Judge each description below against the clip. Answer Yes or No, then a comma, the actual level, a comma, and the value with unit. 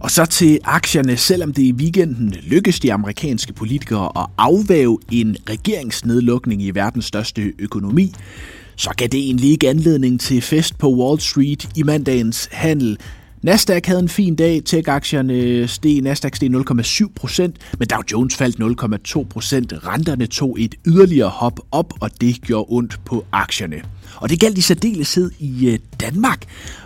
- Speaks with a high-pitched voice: No, low, 125 Hz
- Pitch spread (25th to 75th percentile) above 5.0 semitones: Yes, wide, 5.6 semitones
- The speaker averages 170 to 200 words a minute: No, average, 150 wpm